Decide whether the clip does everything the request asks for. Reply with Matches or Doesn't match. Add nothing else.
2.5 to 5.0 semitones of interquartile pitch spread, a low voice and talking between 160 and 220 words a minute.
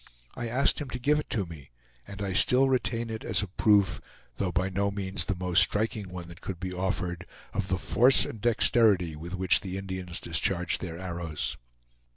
Matches